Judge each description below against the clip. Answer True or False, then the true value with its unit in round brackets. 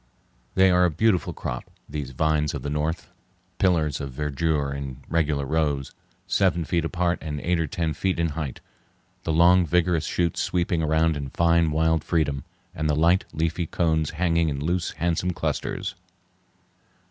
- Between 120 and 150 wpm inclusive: False (160 wpm)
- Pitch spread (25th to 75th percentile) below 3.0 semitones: True (2.4 semitones)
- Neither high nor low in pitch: False (80 Hz)